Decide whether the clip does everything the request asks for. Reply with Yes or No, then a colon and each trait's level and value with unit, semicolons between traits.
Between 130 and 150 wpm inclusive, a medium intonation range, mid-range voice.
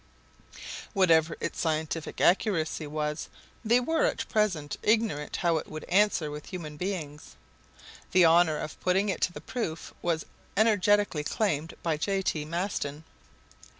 Yes: average, 140 wpm; average, 4.6 semitones; medium, 170 Hz